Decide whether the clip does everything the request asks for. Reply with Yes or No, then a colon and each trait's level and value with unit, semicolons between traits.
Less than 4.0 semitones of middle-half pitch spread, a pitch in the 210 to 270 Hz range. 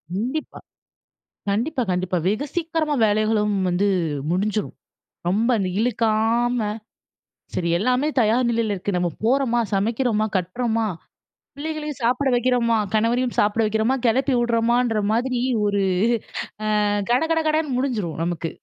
Yes: average, 3.3 semitones; high, 230 Hz